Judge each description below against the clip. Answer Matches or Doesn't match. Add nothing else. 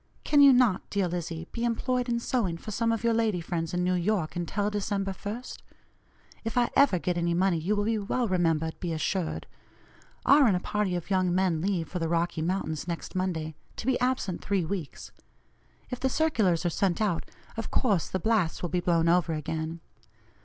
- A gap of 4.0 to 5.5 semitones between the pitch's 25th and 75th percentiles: Matches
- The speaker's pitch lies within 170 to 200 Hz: Matches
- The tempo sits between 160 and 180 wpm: Doesn't match